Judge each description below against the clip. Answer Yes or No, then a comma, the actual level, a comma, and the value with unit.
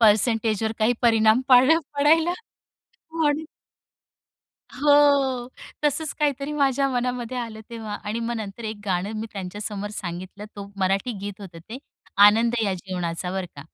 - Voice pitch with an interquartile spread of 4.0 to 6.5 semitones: Yes, average, 4.5 semitones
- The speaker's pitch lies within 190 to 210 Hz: No, high, 225 Hz